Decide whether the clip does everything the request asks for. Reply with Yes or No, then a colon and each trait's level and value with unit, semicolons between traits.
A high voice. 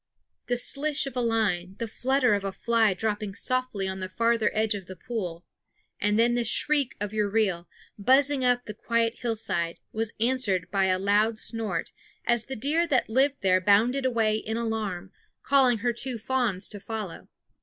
Yes: high, 225 Hz